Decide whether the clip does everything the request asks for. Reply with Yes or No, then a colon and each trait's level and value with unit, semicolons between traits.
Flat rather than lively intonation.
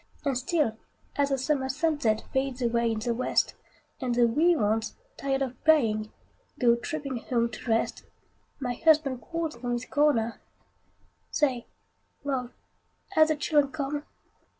No: average, 3.8 semitones